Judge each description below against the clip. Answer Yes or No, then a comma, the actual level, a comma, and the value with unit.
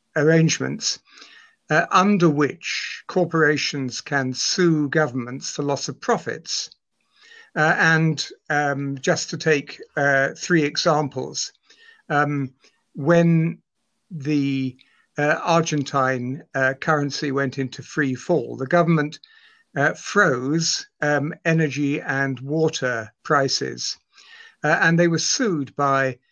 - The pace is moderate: No, slow, 105 wpm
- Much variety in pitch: No, average, 3.4 semitones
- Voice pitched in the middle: Yes, medium, 150 Hz